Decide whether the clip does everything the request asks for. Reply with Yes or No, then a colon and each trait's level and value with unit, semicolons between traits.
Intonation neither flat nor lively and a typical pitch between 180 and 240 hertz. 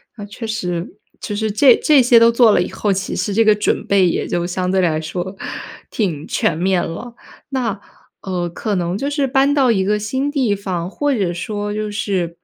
Yes: average, 4.3 semitones; high, 205 Hz